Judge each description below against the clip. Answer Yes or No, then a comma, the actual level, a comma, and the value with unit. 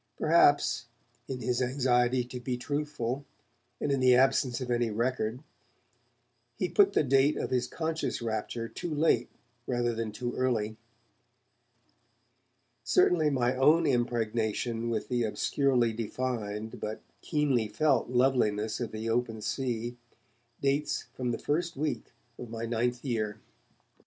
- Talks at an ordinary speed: No, slow, 130 wpm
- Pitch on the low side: Yes, low, 125 Hz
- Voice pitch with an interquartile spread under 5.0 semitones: Yes, average, 2.7 semitones